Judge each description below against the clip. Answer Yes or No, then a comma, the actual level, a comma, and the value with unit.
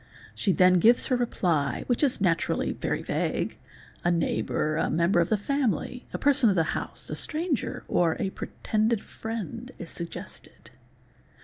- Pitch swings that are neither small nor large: No, wide, 6.2 semitones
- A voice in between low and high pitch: No, high, 205 Hz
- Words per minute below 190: Yes, average, 165 wpm